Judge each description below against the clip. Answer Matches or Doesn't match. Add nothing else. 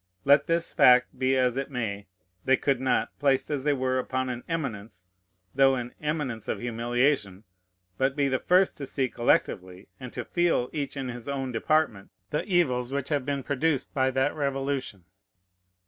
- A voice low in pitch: Matches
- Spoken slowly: Doesn't match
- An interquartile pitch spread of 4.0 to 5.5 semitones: Doesn't match